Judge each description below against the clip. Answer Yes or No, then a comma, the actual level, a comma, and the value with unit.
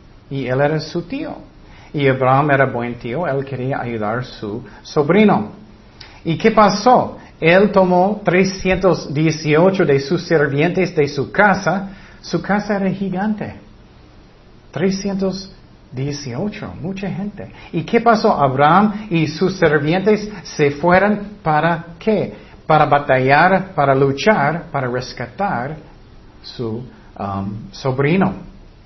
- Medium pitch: Yes, medium, 160 Hz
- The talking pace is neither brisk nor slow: No, slow, 115 wpm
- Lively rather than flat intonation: Yes, wide, 6.0 semitones